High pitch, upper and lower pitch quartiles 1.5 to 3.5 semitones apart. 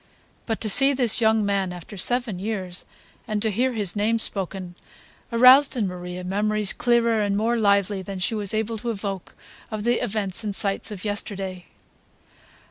Yes: high, 210 Hz; average, 2.8 semitones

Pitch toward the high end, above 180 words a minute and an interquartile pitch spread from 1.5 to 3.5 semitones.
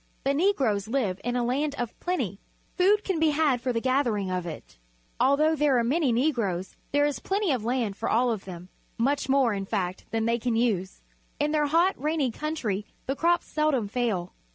No: very high, 250 Hz; average, 200 wpm; wide, 5.6 semitones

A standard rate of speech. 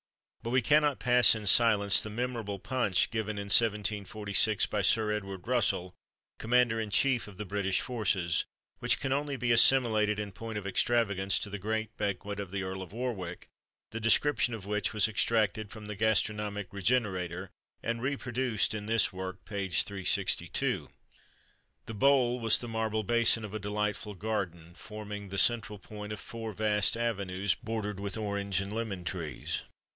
Yes: average, 165 wpm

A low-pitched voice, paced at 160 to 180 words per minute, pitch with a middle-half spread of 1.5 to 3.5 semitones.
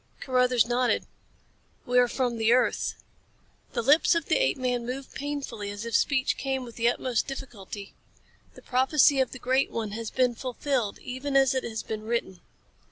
No: very high, 250 Hz; average, 175 wpm; narrow, 2.4 semitones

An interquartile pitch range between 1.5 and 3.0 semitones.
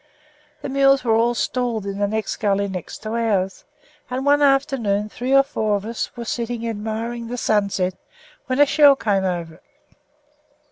No: average, 4.0 semitones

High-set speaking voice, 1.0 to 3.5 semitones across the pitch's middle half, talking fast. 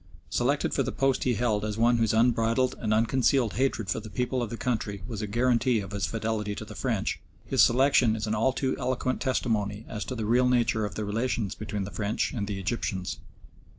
No: low, 115 Hz; average, 2.9 semitones; fast, 220 wpm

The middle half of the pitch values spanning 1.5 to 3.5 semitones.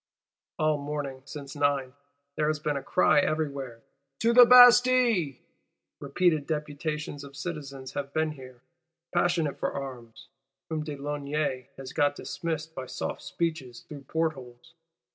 Yes: narrow, 2.6 semitones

